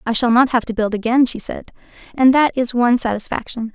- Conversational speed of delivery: No, fast, 225 wpm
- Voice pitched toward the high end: Yes, high, 240 Hz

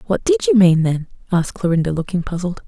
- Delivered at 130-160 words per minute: No, average, 200 wpm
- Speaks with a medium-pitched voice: Yes, medium, 170 Hz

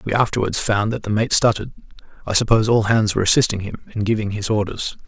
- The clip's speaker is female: No, male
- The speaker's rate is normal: No, fast, 215 wpm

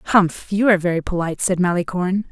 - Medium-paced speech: Yes, average, 180 wpm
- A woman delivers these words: Yes, female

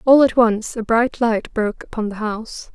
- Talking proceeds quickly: Yes, fast, 220 wpm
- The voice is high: Yes, high, 225 Hz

